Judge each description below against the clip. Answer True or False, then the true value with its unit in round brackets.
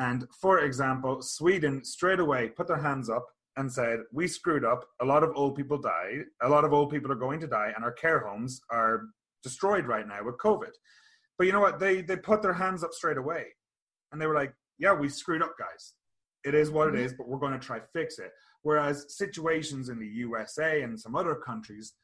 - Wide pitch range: True (5.7 semitones)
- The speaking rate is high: True (225 wpm)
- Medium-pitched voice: True (145 Hz)